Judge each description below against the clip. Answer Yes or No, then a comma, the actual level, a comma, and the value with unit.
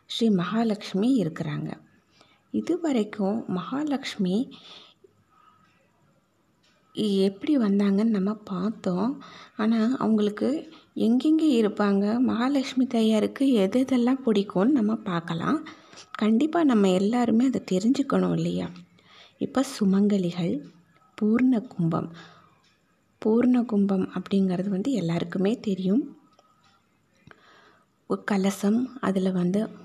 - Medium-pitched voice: No, high, 215 Hz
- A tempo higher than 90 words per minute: No, average, 80 wpm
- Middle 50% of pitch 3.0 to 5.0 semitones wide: Yes, average, 4.7 semitones